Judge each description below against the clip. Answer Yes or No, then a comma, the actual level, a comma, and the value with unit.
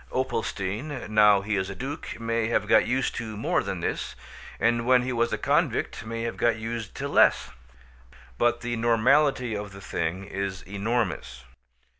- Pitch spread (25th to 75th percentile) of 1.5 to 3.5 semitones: Yes, average, 2.9 semitones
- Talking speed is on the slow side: No, average, 170 wpm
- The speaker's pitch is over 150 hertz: No, low, 115 Hz